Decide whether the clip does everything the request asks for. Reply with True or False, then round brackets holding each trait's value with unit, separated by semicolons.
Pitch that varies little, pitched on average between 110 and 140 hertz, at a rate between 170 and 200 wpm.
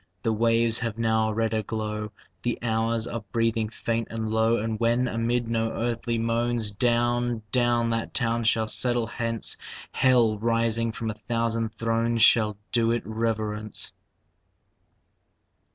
False (0.9 semitones; 115 Hz; 140 wpm)